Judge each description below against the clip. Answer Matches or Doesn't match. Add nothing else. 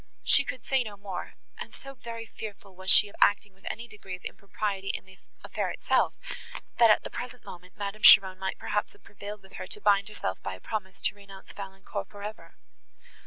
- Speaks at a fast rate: Matches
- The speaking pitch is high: Matches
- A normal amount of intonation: Doesn't match